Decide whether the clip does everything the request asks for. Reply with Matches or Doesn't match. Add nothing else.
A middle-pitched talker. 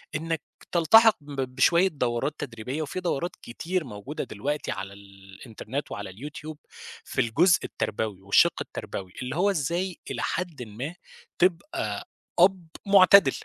Matches